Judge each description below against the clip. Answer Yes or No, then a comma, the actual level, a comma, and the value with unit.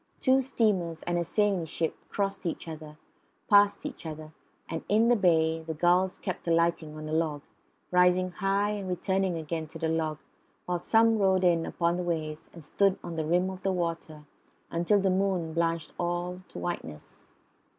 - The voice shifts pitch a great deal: No, average, 2.8 semitones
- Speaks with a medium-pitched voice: Yes, medium, 175 Hz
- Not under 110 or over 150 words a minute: No, average, 175 wpm